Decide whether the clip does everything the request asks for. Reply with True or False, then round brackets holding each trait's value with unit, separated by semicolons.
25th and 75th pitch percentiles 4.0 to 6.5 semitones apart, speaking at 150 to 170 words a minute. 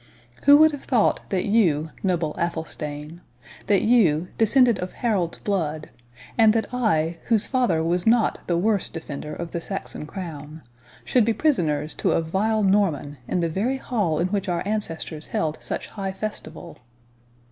True (5.3 semitones; 160 wpm)